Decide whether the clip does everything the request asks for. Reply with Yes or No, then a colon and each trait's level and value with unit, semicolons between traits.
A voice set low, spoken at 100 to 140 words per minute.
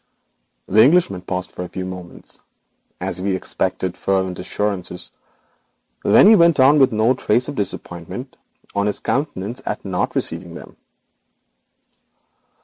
Yes: low, 100 Hz; slow, 135 wpm